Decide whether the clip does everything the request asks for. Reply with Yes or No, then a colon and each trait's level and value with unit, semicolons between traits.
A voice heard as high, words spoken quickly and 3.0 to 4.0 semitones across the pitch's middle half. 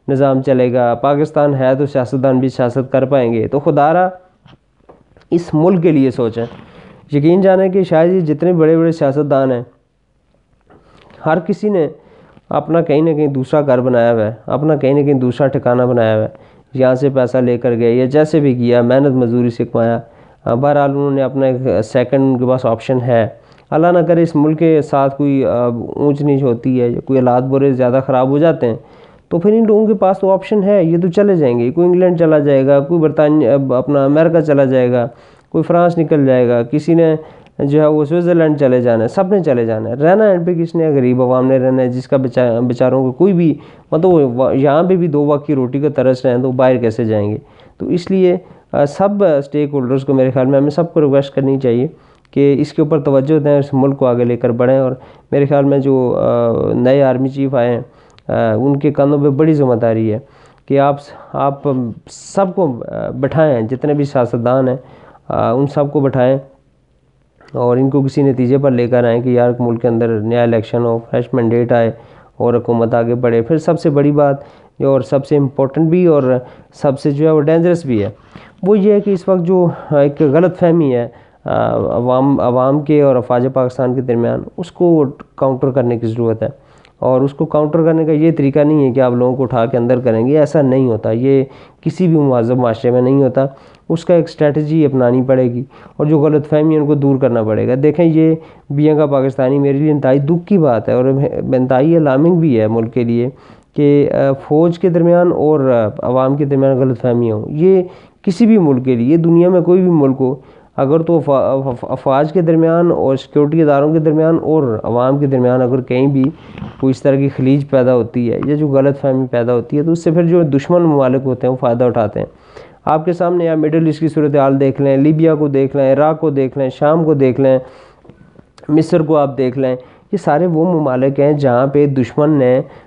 No: medium, 140 Hz; fast, 215 wpm; average, 3.7 semitones